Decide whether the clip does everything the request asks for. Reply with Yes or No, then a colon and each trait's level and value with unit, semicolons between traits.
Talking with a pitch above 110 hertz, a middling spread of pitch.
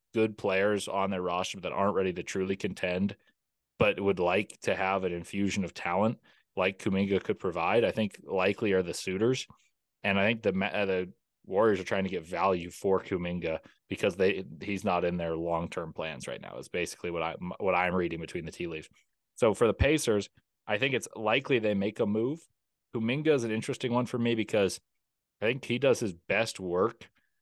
No: low, 100 Hz; average, 3.2 semitones